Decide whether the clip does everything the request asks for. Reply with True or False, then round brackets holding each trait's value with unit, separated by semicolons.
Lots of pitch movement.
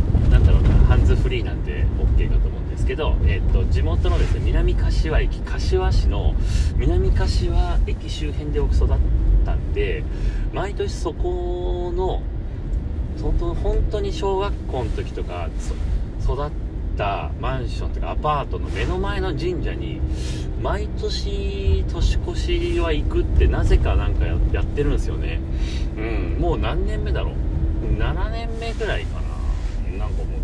False (3.4 semitones)